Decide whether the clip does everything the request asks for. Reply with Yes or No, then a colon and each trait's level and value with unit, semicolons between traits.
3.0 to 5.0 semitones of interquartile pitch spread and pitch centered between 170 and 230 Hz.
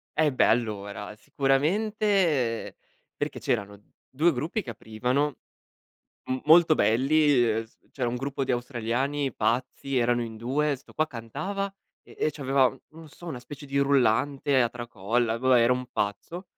No: average, 4.0 semitones; low, 130 Hz